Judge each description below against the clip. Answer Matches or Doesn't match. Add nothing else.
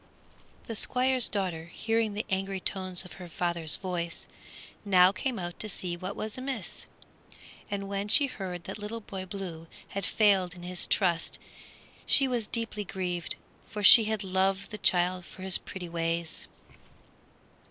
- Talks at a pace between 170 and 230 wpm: Doesn't match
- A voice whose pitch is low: Doesn't match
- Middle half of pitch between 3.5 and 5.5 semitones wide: Doesn't match